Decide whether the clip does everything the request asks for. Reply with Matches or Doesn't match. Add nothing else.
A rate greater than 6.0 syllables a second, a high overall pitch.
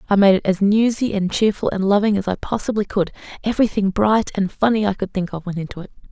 Matches